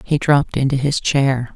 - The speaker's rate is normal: Yes, average, 195 wpm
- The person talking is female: Yes, female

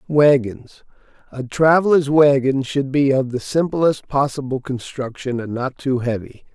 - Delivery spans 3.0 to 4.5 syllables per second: Yes, 4.3 syllables/s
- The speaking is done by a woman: No, male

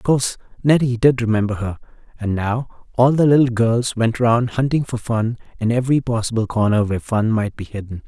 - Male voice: Yes, male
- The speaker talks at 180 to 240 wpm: Yes, average, 195 wpm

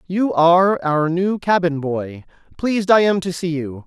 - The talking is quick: No, average, 185 wpm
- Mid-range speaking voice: Yes, medium, 170 Hz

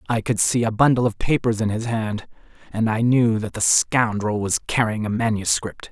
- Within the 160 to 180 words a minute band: No, fast, 205 wpm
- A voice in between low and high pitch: No, low, 110 Hz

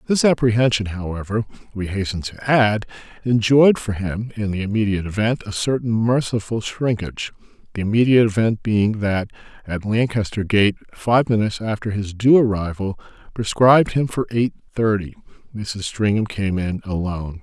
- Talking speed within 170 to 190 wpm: No, average, 145 wpm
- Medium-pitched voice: No, low, 110 Hz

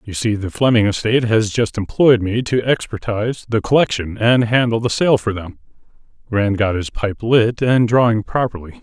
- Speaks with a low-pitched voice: Yes, low, 110 Hz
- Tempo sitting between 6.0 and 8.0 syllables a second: No, 5.0 syllables/s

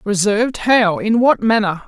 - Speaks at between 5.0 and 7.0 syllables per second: No, 4.6 syllables/s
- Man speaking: No, female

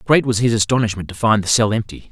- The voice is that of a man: Yes, male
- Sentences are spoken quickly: Yes, fast, 255 wpm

